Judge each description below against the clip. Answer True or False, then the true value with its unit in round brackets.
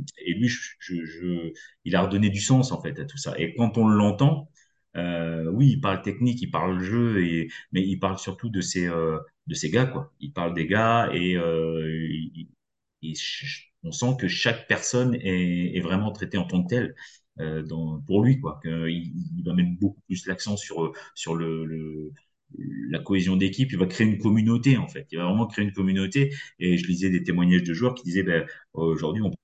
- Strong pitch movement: True (5.7 semitones)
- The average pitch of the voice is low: True (95 Hz)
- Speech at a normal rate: True (210 wpm)